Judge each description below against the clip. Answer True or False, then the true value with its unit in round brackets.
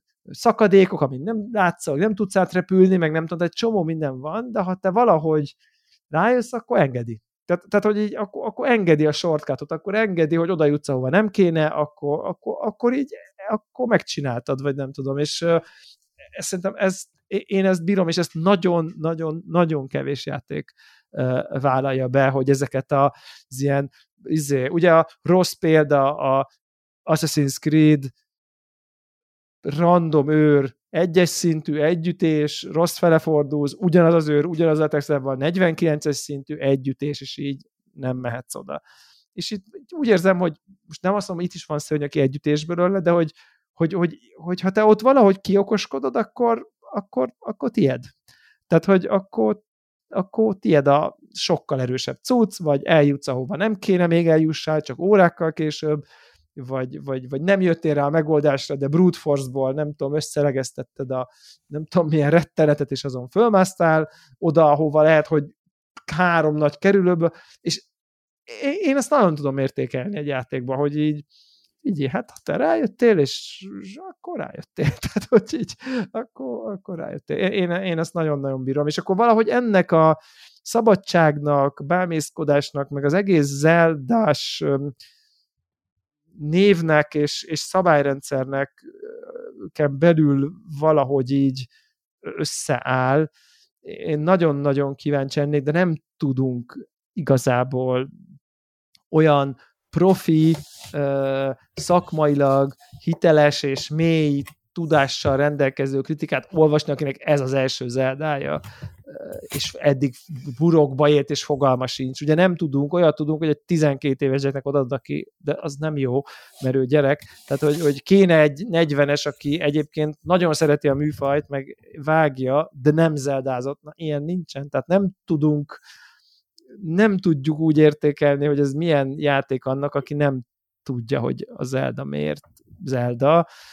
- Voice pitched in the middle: True (155 Hz)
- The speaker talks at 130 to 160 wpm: True (140 wpm)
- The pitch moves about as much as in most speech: True (4.4 semitones)